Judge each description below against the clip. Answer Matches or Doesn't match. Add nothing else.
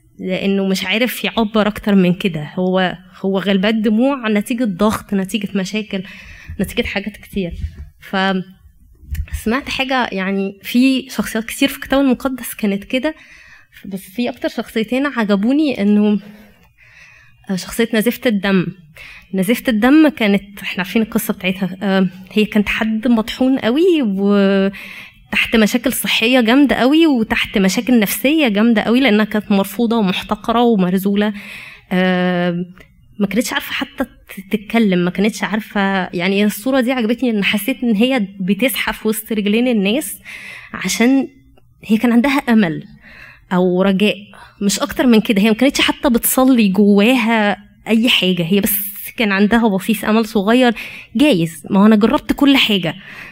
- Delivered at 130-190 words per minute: Matches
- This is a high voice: Matches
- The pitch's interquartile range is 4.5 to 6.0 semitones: Doesn't match